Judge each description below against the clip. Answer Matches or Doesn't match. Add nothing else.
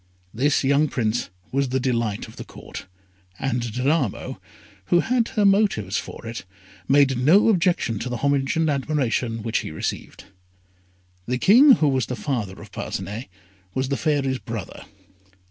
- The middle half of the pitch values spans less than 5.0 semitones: Matches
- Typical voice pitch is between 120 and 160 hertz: Matches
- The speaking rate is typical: Matches